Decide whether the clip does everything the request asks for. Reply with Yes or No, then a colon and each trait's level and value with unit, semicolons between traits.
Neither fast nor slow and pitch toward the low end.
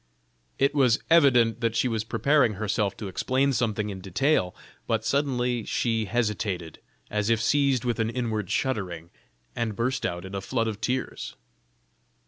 Yes: average, 155 wpm; low, 115 Hz